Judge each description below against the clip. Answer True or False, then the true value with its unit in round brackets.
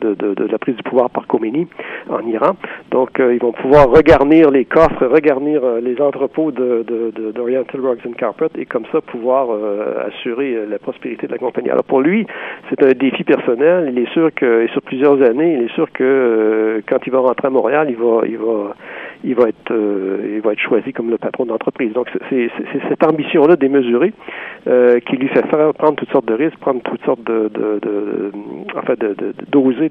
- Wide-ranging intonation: False (4.0 semitones)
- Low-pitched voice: True (130 Hz)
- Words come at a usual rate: False (225 wpm)